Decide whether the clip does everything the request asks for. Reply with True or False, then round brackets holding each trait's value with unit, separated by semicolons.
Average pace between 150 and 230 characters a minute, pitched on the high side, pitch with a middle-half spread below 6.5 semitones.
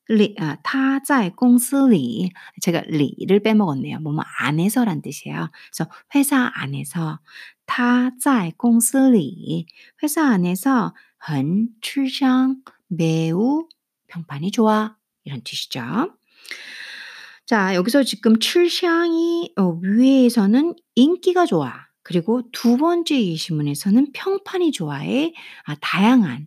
False (220 characters per minute; 230 Hz; 7.3 semitones)